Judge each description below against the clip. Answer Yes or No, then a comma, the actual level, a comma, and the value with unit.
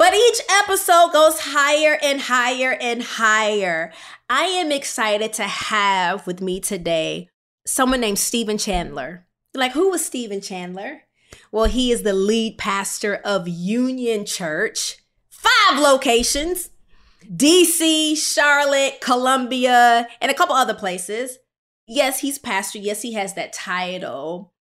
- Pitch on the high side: Yes, high, 240 Hz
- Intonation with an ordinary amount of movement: No, wide, 6.0 semitones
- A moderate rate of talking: No, slow, 130 wpm